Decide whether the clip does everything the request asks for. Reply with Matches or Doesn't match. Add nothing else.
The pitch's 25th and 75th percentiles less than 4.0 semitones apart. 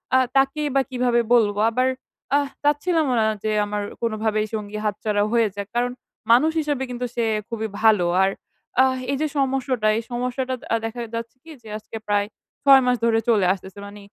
Matches